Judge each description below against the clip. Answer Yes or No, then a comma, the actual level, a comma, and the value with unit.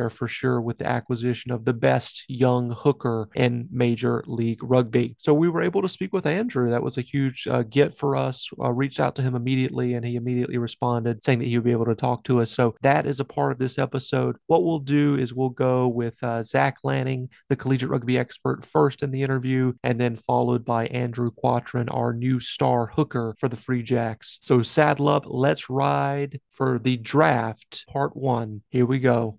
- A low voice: Yes, low, 125 Hz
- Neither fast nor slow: No, fast, 210 wpm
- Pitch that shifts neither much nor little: No, narrow, 2.1 semitones